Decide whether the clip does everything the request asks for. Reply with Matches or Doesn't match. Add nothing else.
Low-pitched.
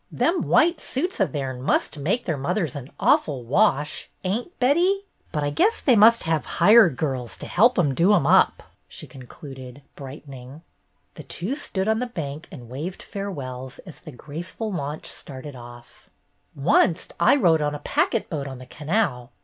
Doesn't match